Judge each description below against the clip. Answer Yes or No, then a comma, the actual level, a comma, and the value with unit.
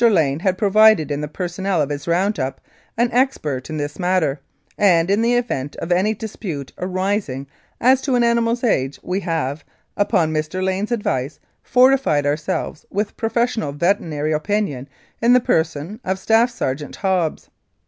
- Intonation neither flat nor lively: No, wide, 6.4 semitones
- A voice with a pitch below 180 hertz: No, medium, 185 Hz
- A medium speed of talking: Yes, average, 160 wpm